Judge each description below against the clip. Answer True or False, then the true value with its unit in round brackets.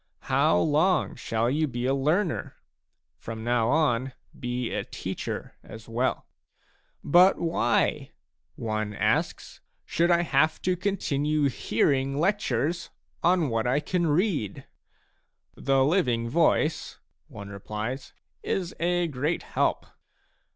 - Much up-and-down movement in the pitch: True (6.0 semitones)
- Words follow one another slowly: True (130 wpm)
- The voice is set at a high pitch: False (140 Hz)